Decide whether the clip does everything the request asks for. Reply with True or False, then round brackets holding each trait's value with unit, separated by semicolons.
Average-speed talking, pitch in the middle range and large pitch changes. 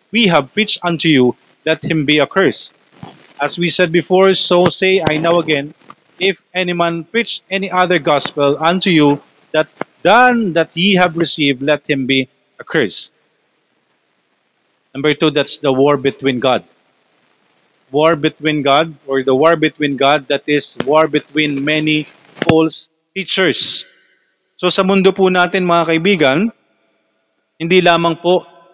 False (145 wpm; 160 Hz; 4.0 semitones)